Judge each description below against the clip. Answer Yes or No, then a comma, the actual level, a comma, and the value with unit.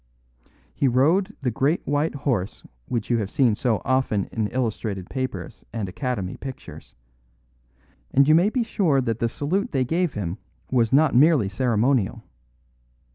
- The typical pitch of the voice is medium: No, low, 130 Hz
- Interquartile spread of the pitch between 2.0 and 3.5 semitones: No, average, 4.7 semitones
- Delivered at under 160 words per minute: Yes, average, 150 wpm